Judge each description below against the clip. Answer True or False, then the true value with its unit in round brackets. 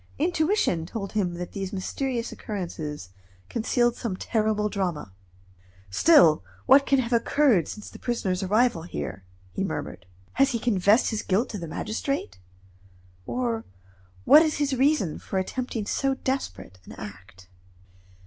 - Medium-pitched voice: False (215 Hz)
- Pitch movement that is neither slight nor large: False (6.5 semitones)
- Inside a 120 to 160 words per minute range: True (140 wpm)